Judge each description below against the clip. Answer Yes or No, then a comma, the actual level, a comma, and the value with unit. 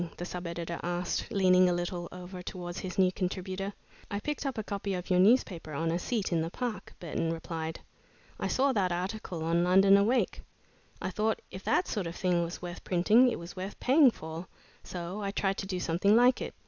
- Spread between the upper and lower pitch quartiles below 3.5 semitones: Yes, average, 2.7 semitones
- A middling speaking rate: No, fast, 210 wpm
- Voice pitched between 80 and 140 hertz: No, medium, 185 Hz